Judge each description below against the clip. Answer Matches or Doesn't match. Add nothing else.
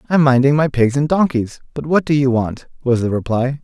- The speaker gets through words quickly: Matches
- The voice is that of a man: Matches